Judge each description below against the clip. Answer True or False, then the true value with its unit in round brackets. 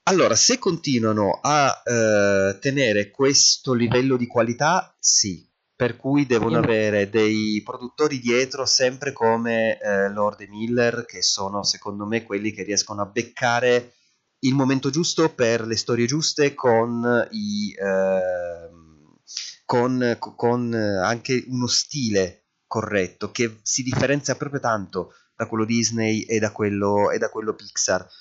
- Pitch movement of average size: True (3.6 semitones)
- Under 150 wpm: True (135 wpm)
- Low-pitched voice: True (115 Hz)